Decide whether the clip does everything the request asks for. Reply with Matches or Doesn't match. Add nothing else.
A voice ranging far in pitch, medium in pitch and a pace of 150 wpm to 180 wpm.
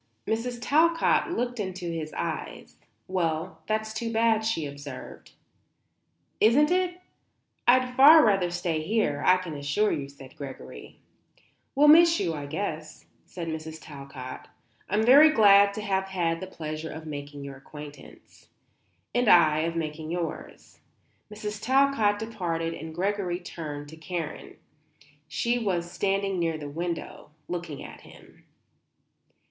Doesn't match